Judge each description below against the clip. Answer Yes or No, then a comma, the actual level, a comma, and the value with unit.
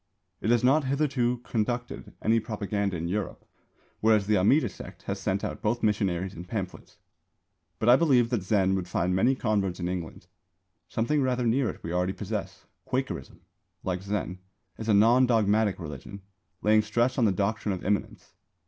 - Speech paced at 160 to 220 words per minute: Yes, average, 170 wpm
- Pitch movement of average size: Yes, average, 3.9 semitones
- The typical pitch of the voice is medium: No, low, 105 Hz